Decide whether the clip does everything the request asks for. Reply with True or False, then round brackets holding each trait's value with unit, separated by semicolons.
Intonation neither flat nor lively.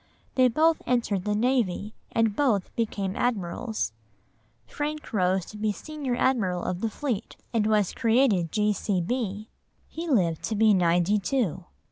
True (4.6 semitones)